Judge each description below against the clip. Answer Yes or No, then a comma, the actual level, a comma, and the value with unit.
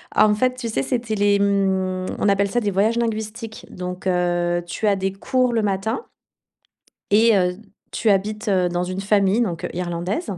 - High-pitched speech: Yes, high, 200 Hz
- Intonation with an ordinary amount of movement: Yes, average, 3.1 semitones